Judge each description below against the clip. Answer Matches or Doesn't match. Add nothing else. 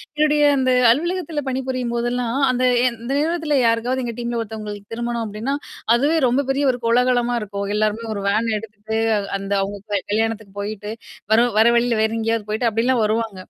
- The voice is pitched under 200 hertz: Doesn't match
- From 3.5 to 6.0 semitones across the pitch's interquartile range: Doesn't match